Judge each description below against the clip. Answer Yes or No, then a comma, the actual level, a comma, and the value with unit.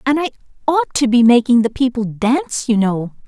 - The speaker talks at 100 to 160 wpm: No, average, 200 wpm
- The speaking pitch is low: No, high, 240 Hz